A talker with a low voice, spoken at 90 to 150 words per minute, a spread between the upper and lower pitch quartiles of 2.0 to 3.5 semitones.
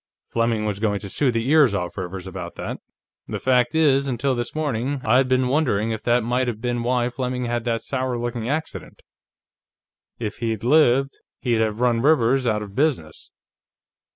No: low, 120 Hz; average, 180 wpm; average, 2.8 semitones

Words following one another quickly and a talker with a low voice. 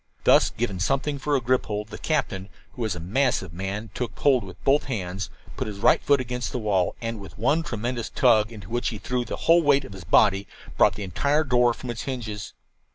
Yes: fast, 225 wpm; low, 115 Hz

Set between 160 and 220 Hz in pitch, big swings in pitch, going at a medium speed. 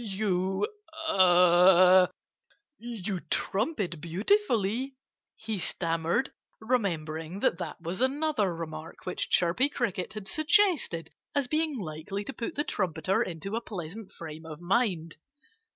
No: high, 190 Hz; wide, 5.7 semitones; slow, 120 wpm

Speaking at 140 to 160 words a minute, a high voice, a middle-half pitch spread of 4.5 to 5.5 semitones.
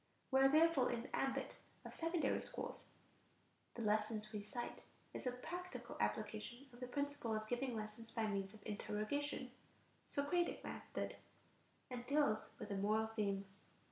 Yes: average, 155 wpm; high, 240 Hz; average, 4.8 semitones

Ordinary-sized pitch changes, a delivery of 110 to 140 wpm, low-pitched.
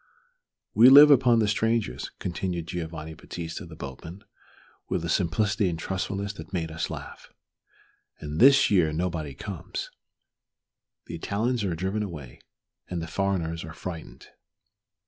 Yes: average, 4.0 semitones; slow, 135 wpm; very low, 90 Hz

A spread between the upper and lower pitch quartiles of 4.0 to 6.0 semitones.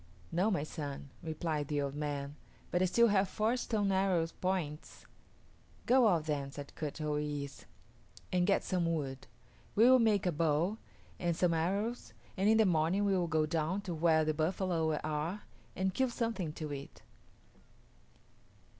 Yes: average, 4.5 semitones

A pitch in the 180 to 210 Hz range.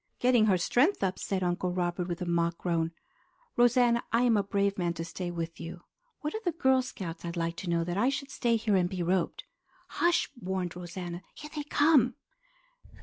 Yes: high, 190 Hz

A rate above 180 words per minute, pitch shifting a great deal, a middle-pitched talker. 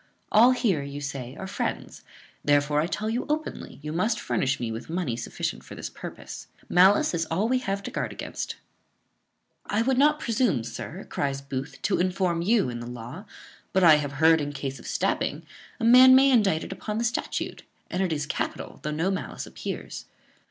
Yes: average, 195 wpm; wide, 7.1 semitones; medium, 175 Hz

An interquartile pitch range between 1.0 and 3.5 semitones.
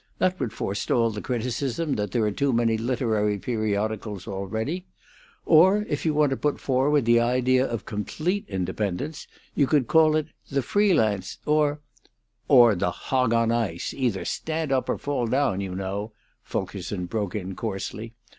No: wide, 5.6 semitones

